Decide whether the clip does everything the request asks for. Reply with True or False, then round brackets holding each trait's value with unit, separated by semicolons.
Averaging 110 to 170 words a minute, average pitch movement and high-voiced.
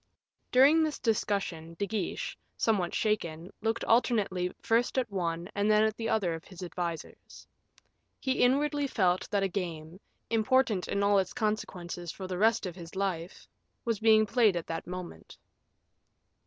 True (155 wpm; 4.2 semitones; 200 Hz)